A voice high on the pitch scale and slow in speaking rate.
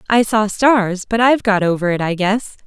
No: high, 210 Hz; fast, 225 wpm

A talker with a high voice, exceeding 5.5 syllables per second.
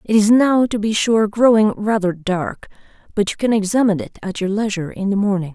Yes: high, 205 Hz; 5.7 syllables/s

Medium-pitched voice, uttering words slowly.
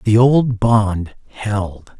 No: low, 110 Hz; slow, 120 wpm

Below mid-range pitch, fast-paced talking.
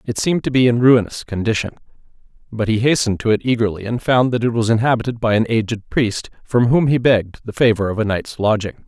Yes: low, 115 Hz; fast, 225 wpm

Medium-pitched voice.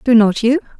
No: high, 235 Hz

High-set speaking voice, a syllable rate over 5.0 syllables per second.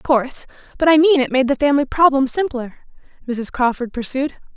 Yes: very high, 270 Hz; 5.8 syllables/s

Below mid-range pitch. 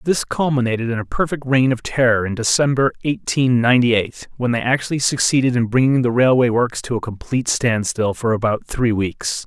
Yes: low, 125 Hz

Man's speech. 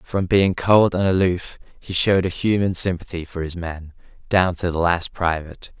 Yes: male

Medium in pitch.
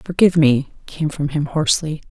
Yes: medium, 150 Hz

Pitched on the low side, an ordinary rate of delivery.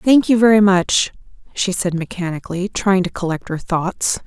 No: high, 190 Hz; average, 170 wpm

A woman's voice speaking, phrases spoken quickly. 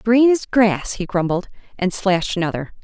No: female; average, 150 wpm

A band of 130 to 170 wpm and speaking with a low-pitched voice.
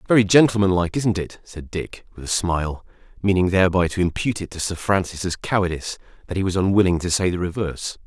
No: average, 200 wpm; very low, 90 Hz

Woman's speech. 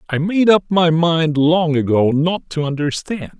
No: male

